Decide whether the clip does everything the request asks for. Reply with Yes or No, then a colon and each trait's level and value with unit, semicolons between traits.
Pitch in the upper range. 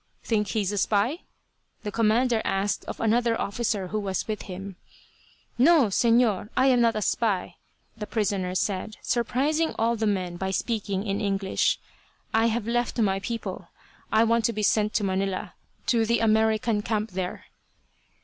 Yes: high, 215 Hz